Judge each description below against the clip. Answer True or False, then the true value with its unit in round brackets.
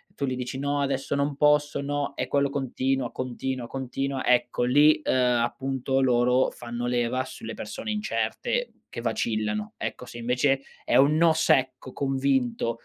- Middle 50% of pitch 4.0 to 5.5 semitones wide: False (2.5 semitones)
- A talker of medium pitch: False (130 Hz)